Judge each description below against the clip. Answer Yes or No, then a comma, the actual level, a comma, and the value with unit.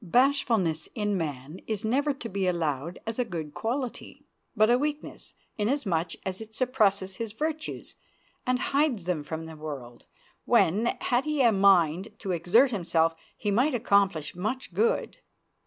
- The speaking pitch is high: Yes, high, 205 Hz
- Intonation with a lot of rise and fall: Yes, wide, 6.5 semitones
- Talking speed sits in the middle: Yes, average, 155 wpm